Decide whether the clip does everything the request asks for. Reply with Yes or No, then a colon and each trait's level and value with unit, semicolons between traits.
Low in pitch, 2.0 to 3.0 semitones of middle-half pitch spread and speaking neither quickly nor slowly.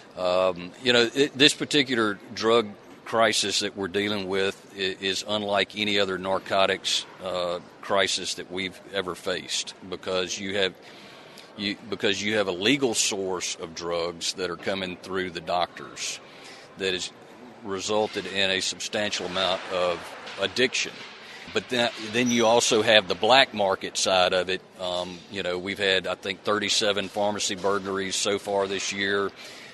Yes: very low, 95 Hz; narrow, 2.4 semitones; average, 155 wpm